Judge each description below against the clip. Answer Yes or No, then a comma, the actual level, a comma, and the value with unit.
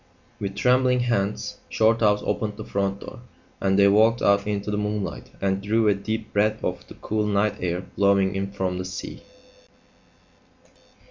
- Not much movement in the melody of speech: Yes, narrow, 1.7 semitones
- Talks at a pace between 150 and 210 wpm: Yes, average, 160 wpm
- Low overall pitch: Yes, low, 105 Hz